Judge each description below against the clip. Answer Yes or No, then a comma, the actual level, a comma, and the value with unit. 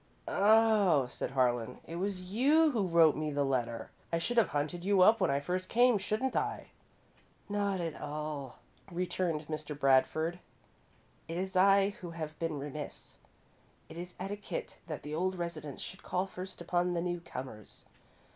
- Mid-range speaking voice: Yes, medium, 170 Hz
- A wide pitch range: No, average, 4.3 semitones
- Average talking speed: Yes, average, 160 wpm